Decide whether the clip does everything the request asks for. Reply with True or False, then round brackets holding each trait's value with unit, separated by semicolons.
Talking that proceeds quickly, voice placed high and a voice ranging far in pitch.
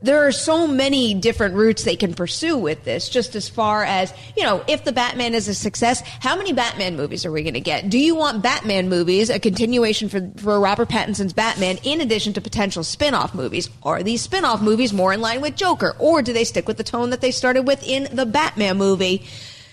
False (225 wpm; 220 Hz; 4.9 semitones)